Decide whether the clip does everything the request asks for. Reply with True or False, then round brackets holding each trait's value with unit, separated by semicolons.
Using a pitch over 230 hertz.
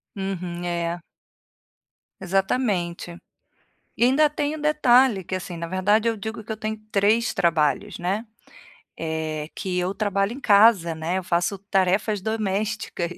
False (195 Hz)